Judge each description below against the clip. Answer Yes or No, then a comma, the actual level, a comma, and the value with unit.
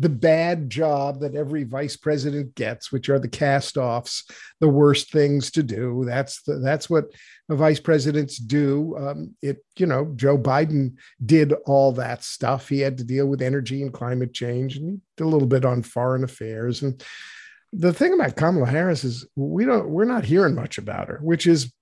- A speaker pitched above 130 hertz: Yes, medium, 140 Hz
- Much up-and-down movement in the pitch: No, average, 2.8 semitones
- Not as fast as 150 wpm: No, average, 195 wpm